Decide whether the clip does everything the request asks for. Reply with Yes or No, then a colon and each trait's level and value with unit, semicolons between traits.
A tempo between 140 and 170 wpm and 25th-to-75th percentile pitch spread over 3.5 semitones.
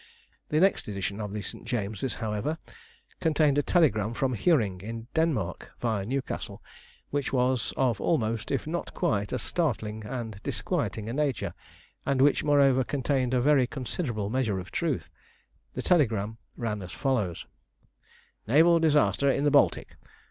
Yes: average, 150 wpm; average, 5.3 semitones